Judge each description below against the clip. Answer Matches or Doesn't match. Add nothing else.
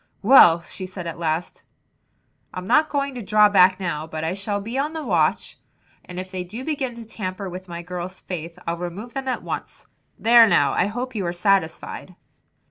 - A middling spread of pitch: Matches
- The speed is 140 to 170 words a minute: Doesn't match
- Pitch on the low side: Doesn't match